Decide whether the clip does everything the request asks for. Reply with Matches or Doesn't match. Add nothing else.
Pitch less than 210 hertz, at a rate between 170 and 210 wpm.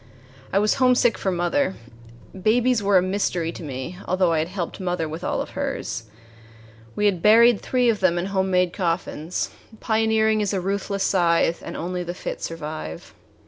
Matches